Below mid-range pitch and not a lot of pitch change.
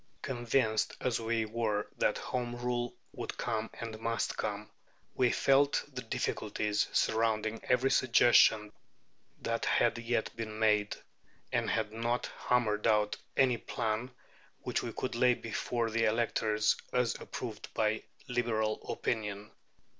Yes: low, 115 Hz; narrow, 2.0 semitones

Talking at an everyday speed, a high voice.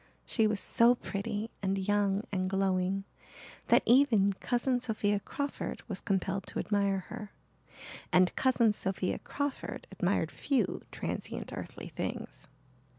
No: slow, 125 wpm; high, 205 Hz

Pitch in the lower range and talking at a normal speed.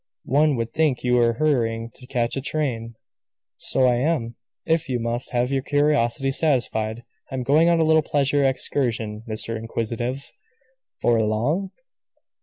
Yes: low, 125 Hz; average, 155 wpm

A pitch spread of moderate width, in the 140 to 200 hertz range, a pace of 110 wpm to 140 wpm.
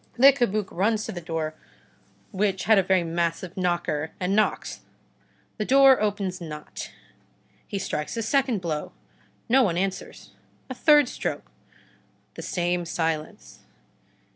Yes: average, 4.5 semitones; high, 190 Hz; slow, 135 wpm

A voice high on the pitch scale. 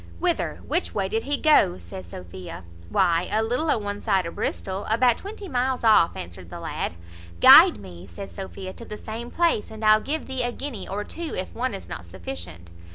Yes: high, 205 Hz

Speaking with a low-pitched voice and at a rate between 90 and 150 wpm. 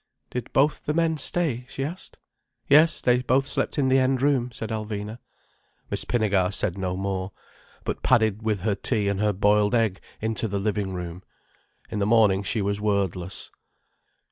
No: low, 110 Hz; average, 170 wpm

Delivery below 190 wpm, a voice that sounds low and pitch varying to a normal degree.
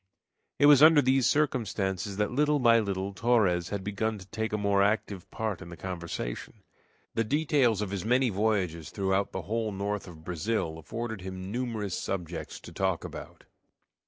Yes: average, 170 wpm; low, 105 Hz; average, 3.5 semitones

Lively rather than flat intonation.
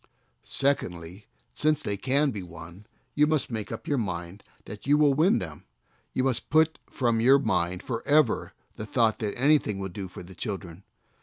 Yes: wide, 6.9 semitones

